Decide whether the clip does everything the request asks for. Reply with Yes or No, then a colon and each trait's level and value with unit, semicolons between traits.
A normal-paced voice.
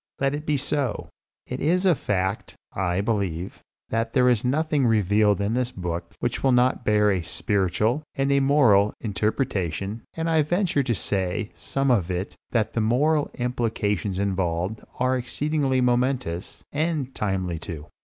Yes: average, 160 wpm